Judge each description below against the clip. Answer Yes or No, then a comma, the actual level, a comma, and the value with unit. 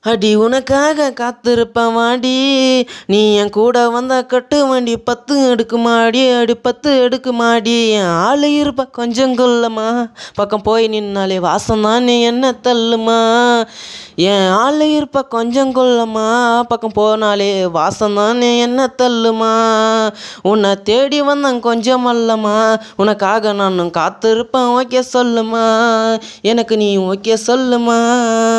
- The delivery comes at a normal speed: Yes, average, 110 wpm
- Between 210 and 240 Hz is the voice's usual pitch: Yes, high, 235 Hz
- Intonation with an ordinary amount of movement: No, narrow, 2.3 semitones